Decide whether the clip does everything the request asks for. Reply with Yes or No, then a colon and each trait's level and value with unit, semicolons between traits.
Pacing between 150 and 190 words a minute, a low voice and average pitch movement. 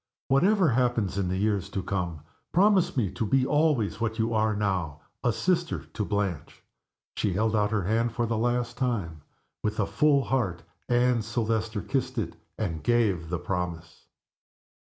Yes: average, 160 wpm; low, 110 Hz; average, 4.1 semitones